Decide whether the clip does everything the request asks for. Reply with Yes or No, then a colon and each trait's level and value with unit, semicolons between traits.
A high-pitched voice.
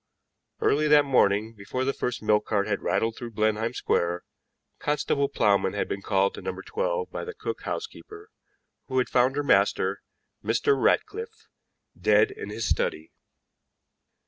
No: low, 130 Hz